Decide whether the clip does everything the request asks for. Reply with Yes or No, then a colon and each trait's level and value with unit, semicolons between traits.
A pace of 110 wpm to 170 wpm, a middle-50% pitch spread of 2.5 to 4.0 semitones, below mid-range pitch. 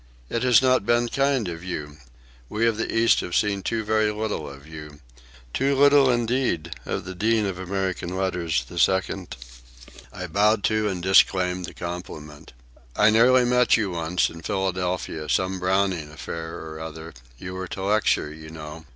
No: average, 165 wpm; average, 5.2 semitones; very low, 95 Hz